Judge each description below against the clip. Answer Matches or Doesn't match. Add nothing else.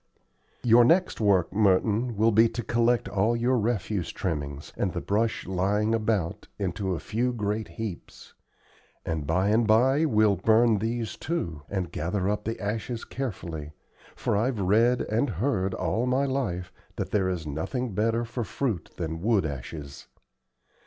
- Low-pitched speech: Matches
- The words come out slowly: Doesn't match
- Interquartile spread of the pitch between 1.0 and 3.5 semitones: Doesn't match